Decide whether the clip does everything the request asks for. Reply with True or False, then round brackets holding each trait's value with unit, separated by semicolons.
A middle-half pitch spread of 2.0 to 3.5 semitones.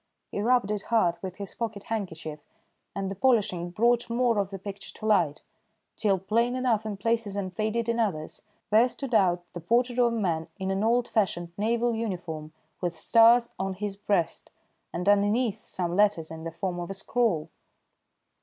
False (4.3 semitones)